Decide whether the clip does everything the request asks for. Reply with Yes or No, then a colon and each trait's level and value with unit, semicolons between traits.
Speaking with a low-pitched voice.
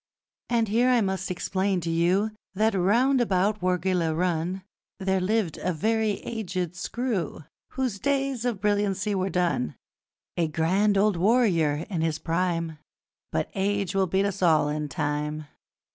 No: high, 190 Hz